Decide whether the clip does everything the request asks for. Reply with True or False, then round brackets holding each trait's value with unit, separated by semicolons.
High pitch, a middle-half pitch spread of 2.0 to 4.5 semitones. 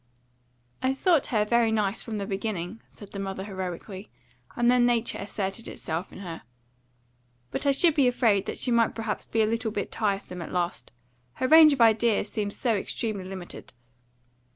True (215 Hz; 3.5 semitones)